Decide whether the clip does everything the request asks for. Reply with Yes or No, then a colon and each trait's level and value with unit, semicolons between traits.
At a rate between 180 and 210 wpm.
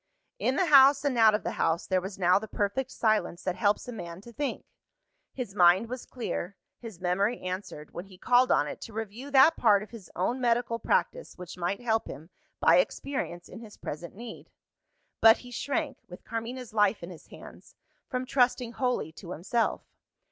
Yes: average, 190 wpm